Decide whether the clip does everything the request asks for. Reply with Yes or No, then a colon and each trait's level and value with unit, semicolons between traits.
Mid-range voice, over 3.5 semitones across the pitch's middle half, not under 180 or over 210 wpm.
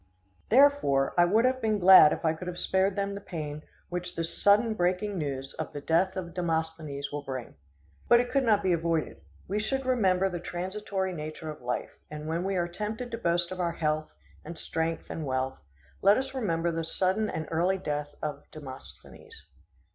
Yes: medium, 175 Hz; average, 4.2 semitones; average, 200 wpm